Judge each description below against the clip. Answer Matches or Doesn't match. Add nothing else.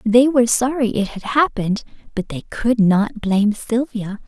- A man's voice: Doesn't match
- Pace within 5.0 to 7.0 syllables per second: Doesn't match